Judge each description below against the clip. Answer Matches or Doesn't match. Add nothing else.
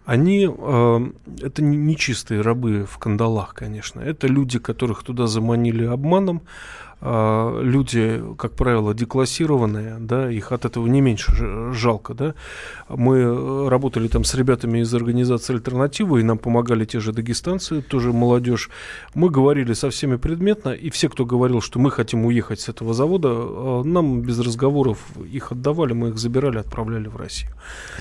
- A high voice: Doesn't match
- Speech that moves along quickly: Doesn't match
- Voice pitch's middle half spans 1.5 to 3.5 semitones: Matches